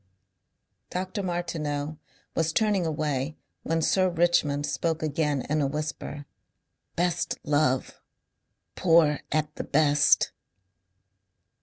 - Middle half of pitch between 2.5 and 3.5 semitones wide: Yes, average, 2.8 semitones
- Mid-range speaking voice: Yes, medium, 155 Hz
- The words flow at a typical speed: No, slow, 95 wpm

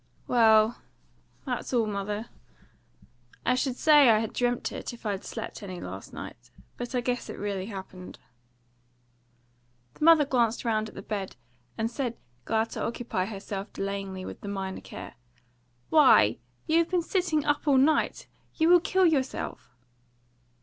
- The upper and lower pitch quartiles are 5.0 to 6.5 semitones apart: Yes, wide, 5.5 semitones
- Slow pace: No, average, 155 wpm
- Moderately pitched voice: No, high, 230 Hz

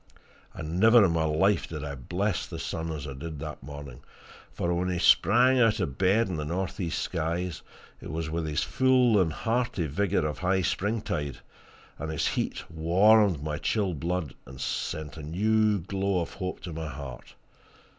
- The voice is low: Yes, very low, 85 Hz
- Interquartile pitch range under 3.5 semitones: No, average, 4.5 semitones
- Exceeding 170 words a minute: Yes, average, 180 wpm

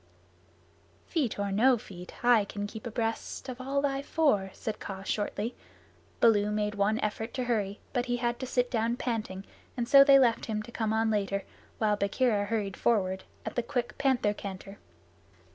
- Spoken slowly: No, average, 175 wpm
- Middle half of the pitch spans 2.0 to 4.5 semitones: Yes, average, 3.2 semitones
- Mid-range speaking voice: No, high, 225 Hz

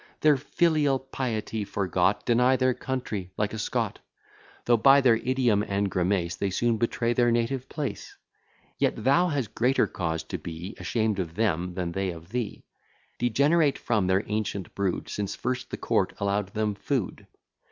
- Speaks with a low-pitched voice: Yes, low, 110 Hz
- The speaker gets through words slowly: No, average, 165 wpm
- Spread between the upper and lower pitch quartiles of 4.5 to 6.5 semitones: Yes, average, 4.8 semitones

